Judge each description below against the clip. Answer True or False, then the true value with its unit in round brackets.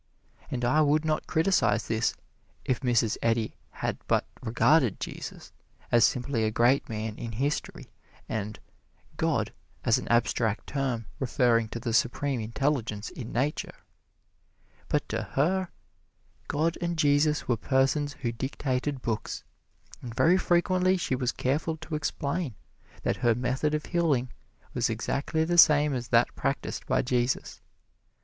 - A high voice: False (130 Hz)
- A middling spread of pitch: True (4.4 semitones)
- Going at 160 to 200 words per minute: False (140 wpm)